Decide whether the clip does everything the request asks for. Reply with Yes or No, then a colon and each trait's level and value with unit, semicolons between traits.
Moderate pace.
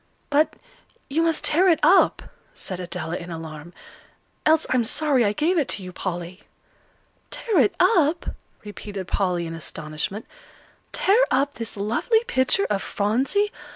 Yes: average, 145 wpm